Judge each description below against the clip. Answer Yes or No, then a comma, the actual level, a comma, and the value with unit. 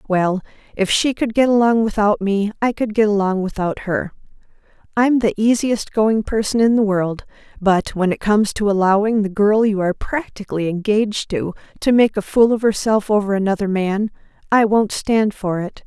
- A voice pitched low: No, high, 210 Hz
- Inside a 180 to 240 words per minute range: Yes, average, 185 wpm